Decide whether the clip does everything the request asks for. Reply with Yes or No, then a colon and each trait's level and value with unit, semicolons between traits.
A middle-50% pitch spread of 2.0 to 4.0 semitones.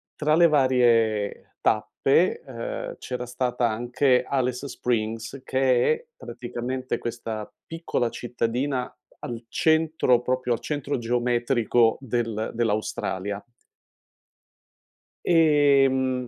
Yes: narrow, 2.6 semitones